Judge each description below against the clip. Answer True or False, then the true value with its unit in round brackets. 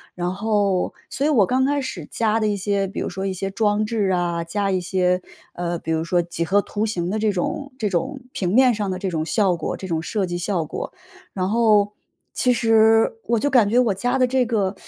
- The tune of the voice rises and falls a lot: False (3.8 semitones)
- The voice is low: False (200 Hz)